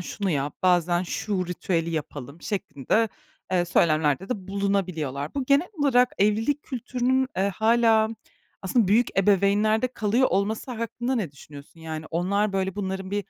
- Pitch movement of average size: Yes, average, 4.5 semitones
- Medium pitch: No, high, 200 Hz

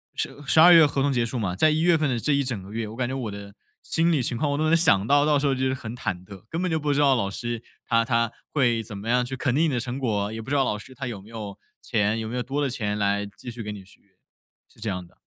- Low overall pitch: Yes, low, 120 Hz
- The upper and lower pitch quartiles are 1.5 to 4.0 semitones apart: No, average, 5.0 semitones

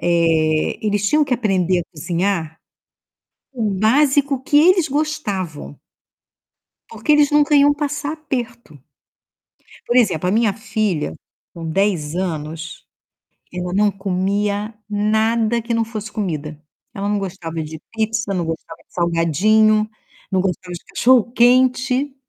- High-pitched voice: Yes, high, 205 Hz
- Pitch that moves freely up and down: Yes, wide, 5.9 semitones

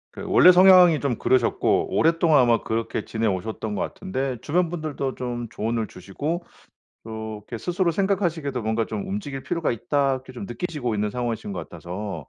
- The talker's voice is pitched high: No, low, 130 Hz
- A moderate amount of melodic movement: No, wide, 7.2 semitones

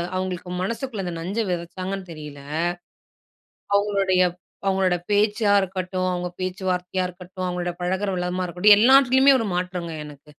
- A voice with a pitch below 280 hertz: Yes, medium, 185 Hz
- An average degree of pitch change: No, narrow, 2.2 semitones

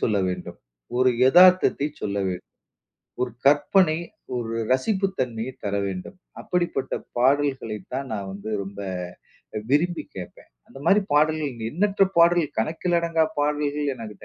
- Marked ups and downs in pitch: Yes, wide, 6.7 semitones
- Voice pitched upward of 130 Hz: Yes, medium, 140 Hz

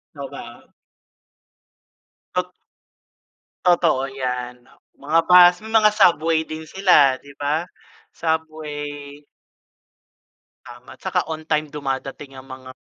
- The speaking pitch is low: No, medium, 150 Hz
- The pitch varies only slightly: No, average, 3.5 semitones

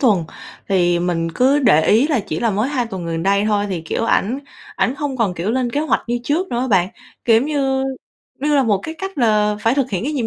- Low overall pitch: No, high, 230 Hz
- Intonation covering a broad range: Yes, wide, 5.7 semitones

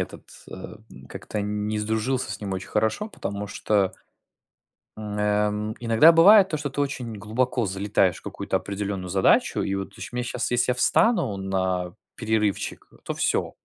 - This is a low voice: Yes, low, 105 Hz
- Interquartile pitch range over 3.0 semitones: Yes, average, 3.7 semitones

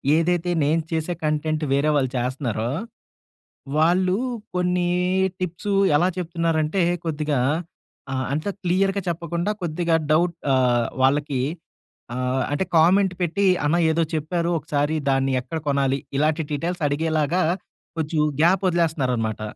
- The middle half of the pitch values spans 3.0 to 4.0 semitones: Yes, average, 3.4 semitones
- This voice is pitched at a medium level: Yes, medium, 160 Hz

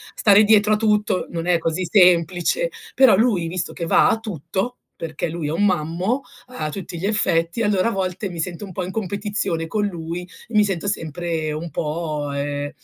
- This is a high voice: No, medium, 180 Hz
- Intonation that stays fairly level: No, average, 3.9 semitones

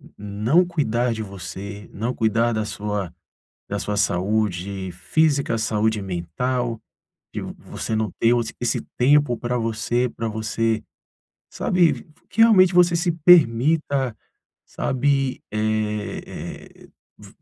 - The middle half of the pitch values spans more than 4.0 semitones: Yes, average, 4.6 semitones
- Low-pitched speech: Yes, low, 115 Hz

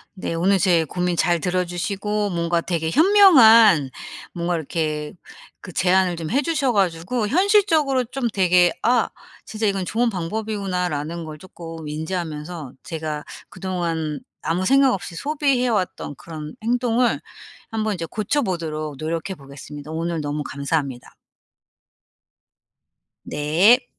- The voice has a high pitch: No, medium, 180 Hz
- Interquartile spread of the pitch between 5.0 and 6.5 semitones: Yes, wide, 5.5 semitones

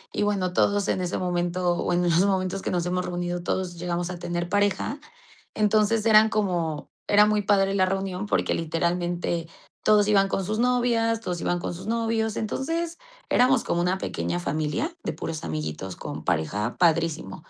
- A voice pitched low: No, medium, 185 Hz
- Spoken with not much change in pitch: No, average, 3.3 semitones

